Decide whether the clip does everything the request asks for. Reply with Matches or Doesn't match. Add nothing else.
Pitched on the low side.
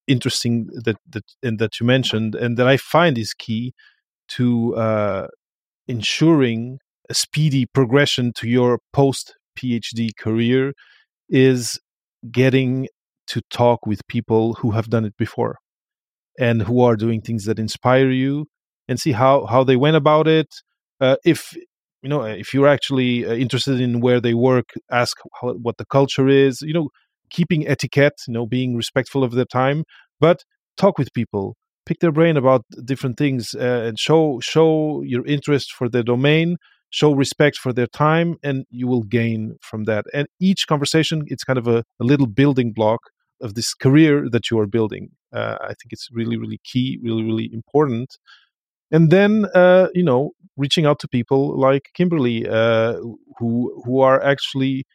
Matches